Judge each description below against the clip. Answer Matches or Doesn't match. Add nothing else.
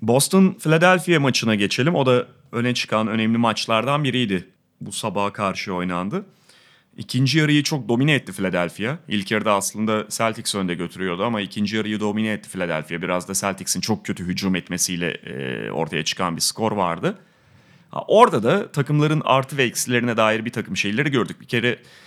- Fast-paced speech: Matches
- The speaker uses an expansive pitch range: Doesn't match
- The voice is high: Doesn't match